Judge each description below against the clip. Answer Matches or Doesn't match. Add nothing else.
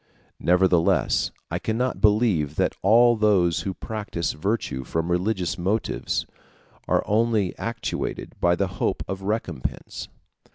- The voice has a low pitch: Matches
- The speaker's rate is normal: Doesn't match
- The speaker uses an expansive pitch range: Doesn't match